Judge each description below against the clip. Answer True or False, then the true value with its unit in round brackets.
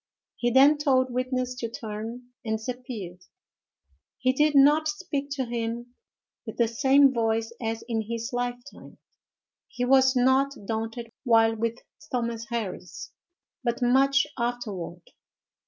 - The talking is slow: True (125 wpm)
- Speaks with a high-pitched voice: True (245 Hz)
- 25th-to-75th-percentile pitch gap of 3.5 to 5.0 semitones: False (2.6 semitones)